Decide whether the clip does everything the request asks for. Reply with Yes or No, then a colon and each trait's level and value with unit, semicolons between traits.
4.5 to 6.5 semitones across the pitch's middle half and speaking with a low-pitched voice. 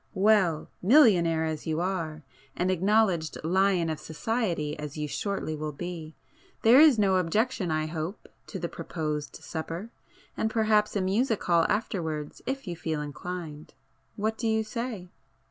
No: average, 5.2 semitones; medium, 180 Hz